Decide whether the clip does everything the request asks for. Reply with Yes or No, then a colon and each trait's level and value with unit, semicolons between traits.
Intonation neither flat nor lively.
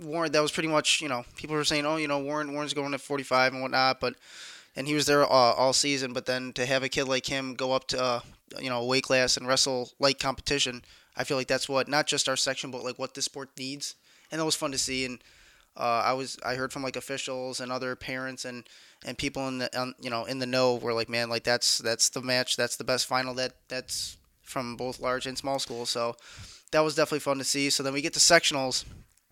No: narrow, 1.8 semitones